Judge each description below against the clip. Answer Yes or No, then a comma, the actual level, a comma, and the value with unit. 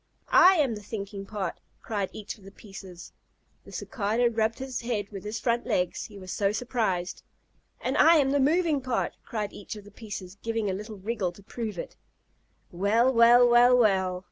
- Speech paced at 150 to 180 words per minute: No, average, 190 wpm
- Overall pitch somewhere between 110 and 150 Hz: No, high, 215 Hz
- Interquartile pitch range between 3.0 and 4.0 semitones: Yes, average, 3.4 semitones